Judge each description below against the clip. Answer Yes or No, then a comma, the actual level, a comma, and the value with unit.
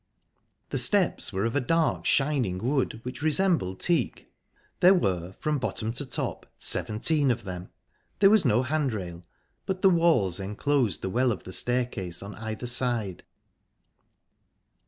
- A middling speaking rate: Yes, average, 145 wpm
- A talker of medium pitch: No, low, 125 Hz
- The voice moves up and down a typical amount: No, wide, 7.2 semitones